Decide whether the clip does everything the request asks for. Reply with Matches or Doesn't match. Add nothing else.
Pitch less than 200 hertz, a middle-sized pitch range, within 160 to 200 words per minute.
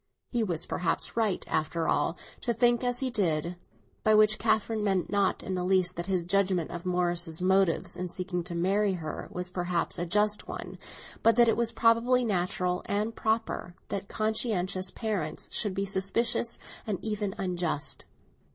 Matches